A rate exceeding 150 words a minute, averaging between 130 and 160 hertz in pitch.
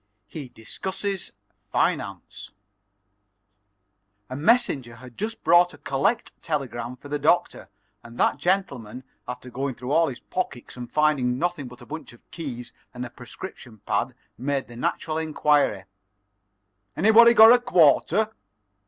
No: average, 140 wpm; medium, 140 Hz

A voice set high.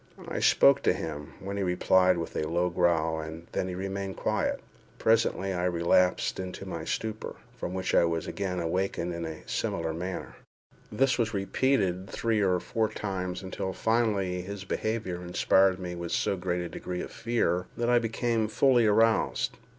No: very low, 95 Hz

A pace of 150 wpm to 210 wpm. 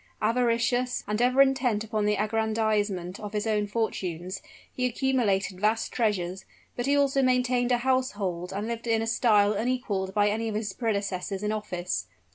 Yes: average, 165 wpm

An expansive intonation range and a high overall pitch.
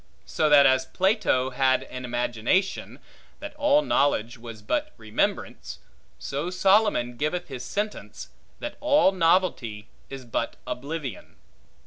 No: wide, 7.7 semitones; medium, 145 Hz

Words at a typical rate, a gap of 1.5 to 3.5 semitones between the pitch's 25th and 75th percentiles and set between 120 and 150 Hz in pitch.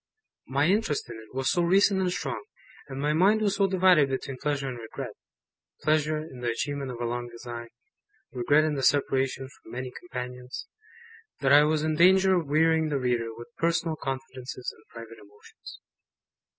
No: average, 175 wpm; average, 4.4 semitones; medium, 140 Hz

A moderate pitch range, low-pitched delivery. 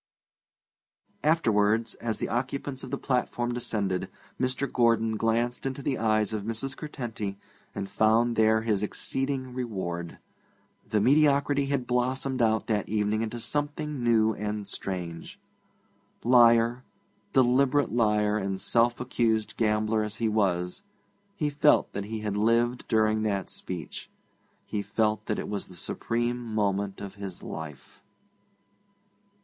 Yes: average, 3.0 semitones; low, 110 Hz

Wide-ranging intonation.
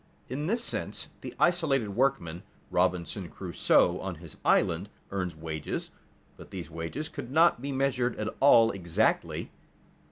Yes: wide, 8.0 semitones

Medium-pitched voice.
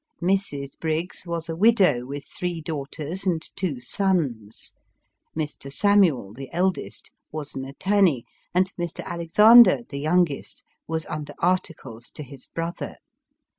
Yes: medium, 165 Hz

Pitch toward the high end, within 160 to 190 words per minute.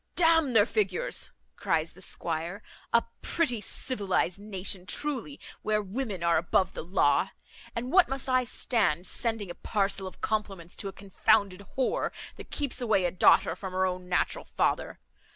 Yes: high, 205 Hz; average, 165 wpm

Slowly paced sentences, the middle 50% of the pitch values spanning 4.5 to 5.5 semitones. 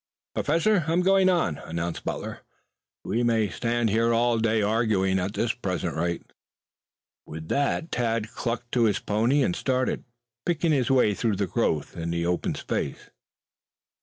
No: average, 155 wpm; average, 5.2 semitones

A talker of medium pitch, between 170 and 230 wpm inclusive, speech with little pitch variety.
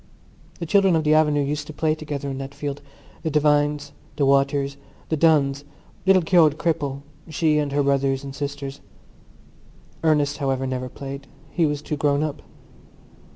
No: medium, 145 Hz; average, 160 wpm; narrow, 1.8 semitones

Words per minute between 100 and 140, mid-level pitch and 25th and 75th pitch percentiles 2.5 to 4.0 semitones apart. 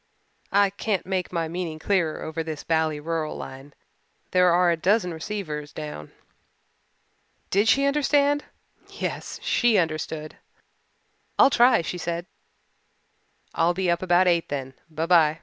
Yes: slow, 135 wpm; medium, 170 Hz; average, 3.6 semitones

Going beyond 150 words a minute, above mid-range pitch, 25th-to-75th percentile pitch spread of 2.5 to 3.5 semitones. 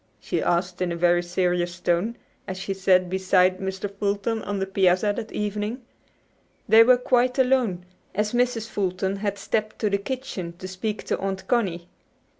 Yes: average, 170 wpm; high, 195 Hz; average, 3.0 semitones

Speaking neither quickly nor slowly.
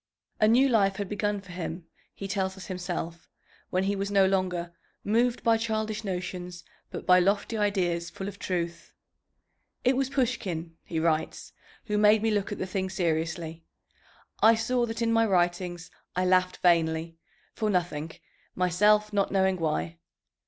Yes: average, 160 wpm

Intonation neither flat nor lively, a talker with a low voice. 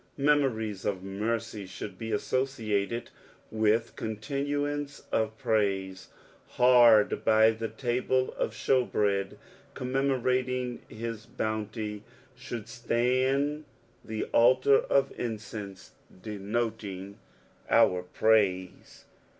Yes: average, 3.4 semitones; low, 110 Hz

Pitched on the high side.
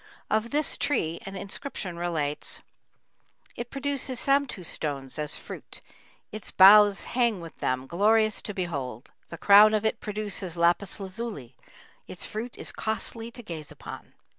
Yes: high, 200 Hz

